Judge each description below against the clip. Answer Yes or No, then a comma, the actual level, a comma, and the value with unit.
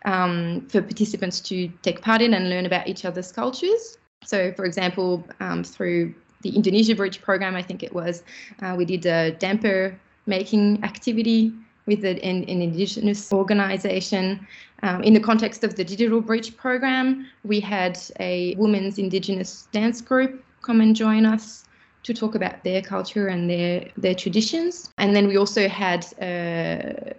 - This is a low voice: No, high, 195 Hz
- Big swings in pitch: No, average, 3.3 semitones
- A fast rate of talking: No, average, 160 wpm